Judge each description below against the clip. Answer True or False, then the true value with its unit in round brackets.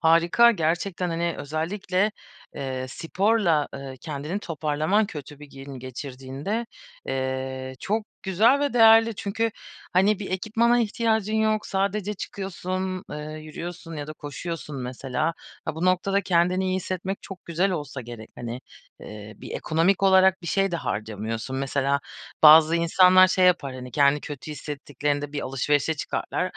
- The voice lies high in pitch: False (165 Hz)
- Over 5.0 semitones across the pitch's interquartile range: True (5.6 semitones)